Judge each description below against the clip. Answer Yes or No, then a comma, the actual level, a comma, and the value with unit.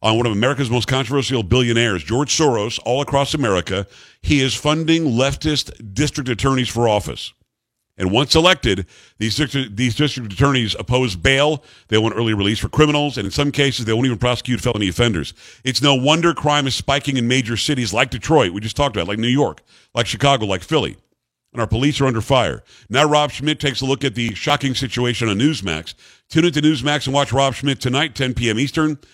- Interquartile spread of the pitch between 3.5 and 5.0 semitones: Yes, average, 4.0 semitones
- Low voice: Yes, low, 130 Hz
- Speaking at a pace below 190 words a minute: No, average, 200 wpm